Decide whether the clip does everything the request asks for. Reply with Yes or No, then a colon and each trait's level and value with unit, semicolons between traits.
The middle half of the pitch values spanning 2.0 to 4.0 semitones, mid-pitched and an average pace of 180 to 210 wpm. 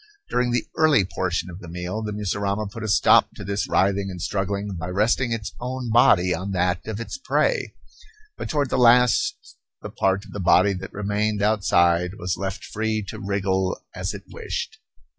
No: average, 2.9 semitones; low, 100 Hz; average, 185 wpm